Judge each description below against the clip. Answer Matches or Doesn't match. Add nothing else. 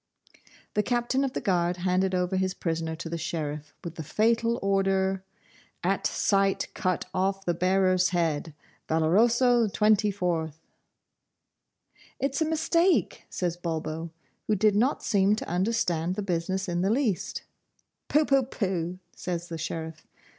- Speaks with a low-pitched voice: Doesn't match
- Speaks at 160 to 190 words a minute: Doesn't match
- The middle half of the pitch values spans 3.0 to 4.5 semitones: Matches